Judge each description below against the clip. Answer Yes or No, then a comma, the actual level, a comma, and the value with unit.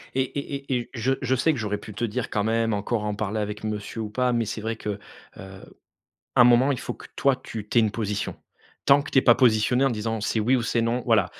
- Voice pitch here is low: Yes, low, 115 Hz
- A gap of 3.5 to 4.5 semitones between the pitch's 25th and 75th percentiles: No, average, 2.9 semitones